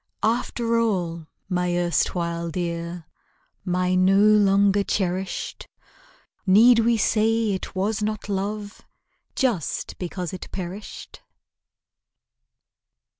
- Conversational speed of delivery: No, slow, 90 wpm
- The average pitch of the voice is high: Yes, high, 195 Hz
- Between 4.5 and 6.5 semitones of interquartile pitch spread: No, average, 3.1 semitones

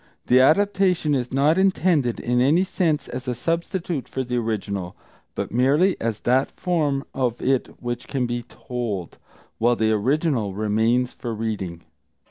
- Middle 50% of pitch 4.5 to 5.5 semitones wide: Yes, average, 5.0 semitones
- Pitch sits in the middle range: No, low, 125 Hz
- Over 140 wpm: Yes, average, 150 wpm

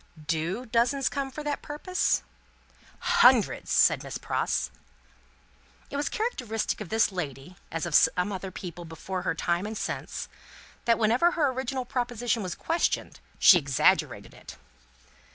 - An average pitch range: No, wide, 7.0 semitones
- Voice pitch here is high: Yes, high, 220 Hz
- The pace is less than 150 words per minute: Yes, average, 140 wpm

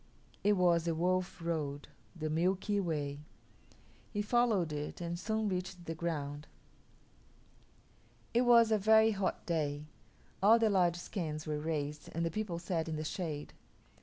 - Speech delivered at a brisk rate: No, average, 150 wpm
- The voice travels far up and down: No, average, 4.5 semitones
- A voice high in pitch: No, medium, 170 Hz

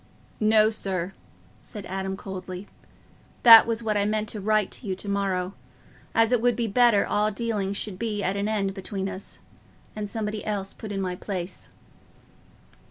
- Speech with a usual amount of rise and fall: No, narrow, 2.0 semitones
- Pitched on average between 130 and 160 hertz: No, high, 205 Hz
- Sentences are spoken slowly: No, average, 170 wpm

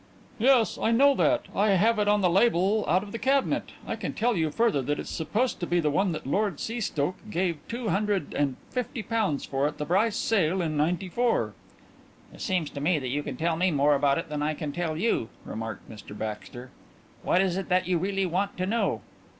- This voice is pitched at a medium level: Yes, medium, 180 Hz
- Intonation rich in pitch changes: Yes, wide, 6.1 semitones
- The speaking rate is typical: No, fast, 215 wpm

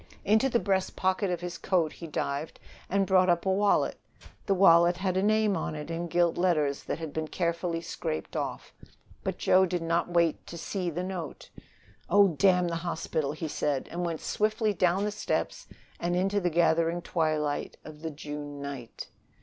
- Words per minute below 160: No, average, 190 wpm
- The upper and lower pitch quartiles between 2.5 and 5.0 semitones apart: Yes, average, 2.9 semitones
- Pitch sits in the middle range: Yes, medium, 175 Hz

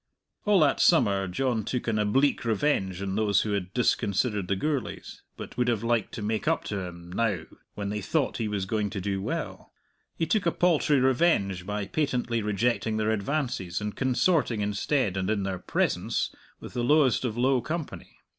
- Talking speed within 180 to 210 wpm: Yes, average, 185 wpm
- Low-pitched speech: Yes, low, 110 Hz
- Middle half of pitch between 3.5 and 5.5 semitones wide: Yes, average, 4.9 semitones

